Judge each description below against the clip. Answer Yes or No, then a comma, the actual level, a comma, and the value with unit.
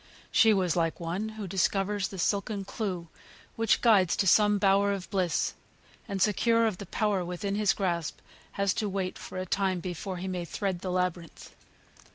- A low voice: No, high, 195 Hz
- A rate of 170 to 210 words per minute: Yes, average, 180 wpm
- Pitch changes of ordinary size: No, narrow, 2.2 semitones